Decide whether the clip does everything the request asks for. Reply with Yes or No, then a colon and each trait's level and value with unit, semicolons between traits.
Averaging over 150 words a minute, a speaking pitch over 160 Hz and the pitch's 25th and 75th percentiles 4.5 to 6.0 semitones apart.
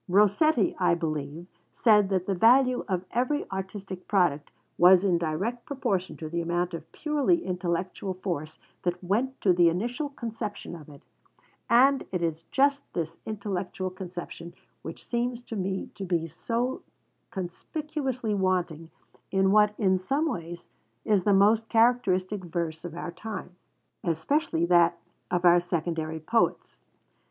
No: average, 145 wpm; medium, 185 Hz; average, 4.9 semitones